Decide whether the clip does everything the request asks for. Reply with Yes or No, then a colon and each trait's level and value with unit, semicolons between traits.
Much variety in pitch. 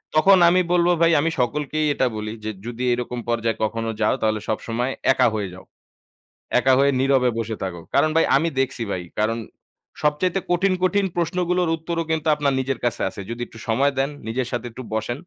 Yes: wide, 6.1 semitones